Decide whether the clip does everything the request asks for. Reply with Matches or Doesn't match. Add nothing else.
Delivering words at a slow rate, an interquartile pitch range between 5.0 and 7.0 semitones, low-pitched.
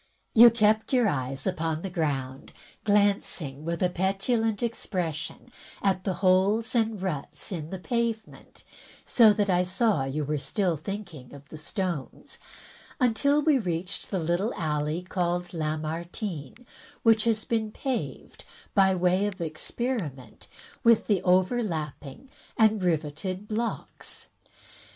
Doesn't match